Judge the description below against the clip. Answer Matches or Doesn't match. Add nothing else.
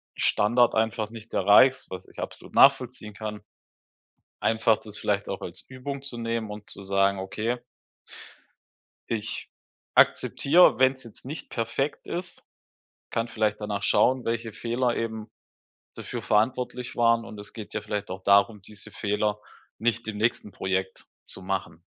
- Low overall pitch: Matches